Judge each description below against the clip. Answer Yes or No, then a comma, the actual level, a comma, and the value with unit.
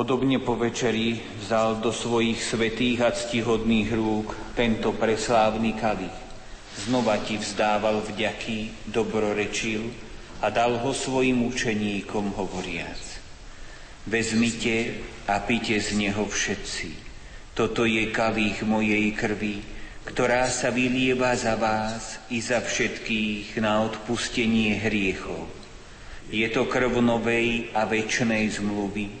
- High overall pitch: No, low, 110 Hz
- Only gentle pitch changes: Yes, narrow, 1.8 semitones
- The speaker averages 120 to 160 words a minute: No, slow, 110 wpm